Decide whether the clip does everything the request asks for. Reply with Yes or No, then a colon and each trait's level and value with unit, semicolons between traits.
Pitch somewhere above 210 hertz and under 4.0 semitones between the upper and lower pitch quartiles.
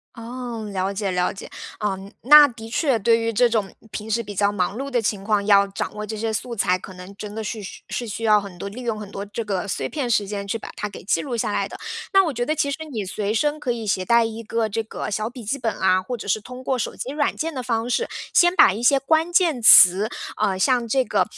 Yes: high, 220 Hz; average, 3.6 semitones